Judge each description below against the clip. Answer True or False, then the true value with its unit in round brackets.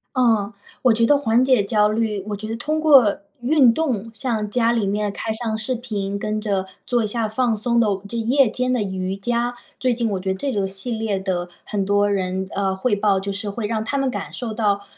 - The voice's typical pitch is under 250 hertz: True (220 Hz)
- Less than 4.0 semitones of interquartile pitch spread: True (3.2 semitones)